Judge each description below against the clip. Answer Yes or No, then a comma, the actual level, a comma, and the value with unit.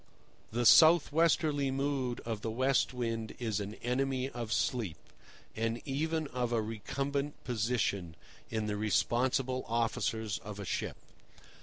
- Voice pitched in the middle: No, low, 120 Hz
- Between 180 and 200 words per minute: No, slow, 135 wpm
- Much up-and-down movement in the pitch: No, average, 3.5 semitones